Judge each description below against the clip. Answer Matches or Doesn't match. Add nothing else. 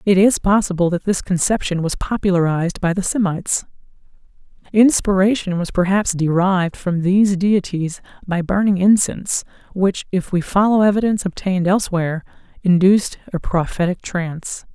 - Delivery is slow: Matches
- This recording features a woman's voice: Matches